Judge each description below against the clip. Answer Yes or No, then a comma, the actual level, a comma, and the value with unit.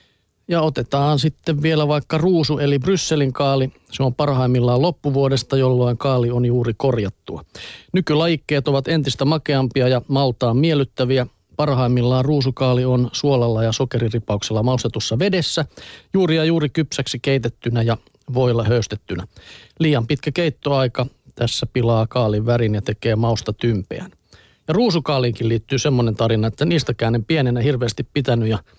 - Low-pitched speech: Yes, low, 130 Hz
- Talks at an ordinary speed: Yes, average, 135 wpm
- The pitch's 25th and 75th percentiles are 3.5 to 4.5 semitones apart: Yes, average, 4.1 semitones